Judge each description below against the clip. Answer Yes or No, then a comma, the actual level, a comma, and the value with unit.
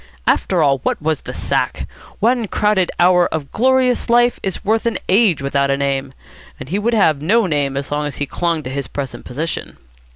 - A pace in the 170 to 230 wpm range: Yes, average, 200 wpm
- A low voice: No, medium, 165 Hz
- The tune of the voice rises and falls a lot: Yes, wide, 7.3 semitones